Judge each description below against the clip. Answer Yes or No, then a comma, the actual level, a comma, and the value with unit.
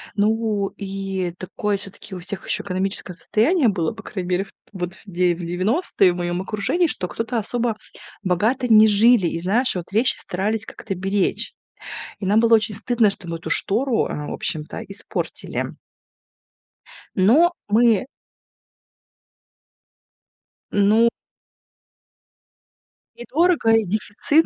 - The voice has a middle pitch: No, high, 205 Hz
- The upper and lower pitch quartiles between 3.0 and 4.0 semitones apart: Yes, average, 3.5 semitones